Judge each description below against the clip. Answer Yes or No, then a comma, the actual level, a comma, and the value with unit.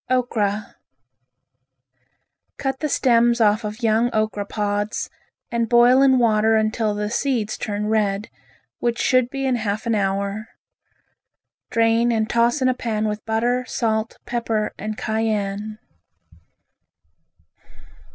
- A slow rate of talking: Yes, slow, 120 wpm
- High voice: Yes, high, 220 Hz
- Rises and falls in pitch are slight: Yes, narrow, 2.1 semitones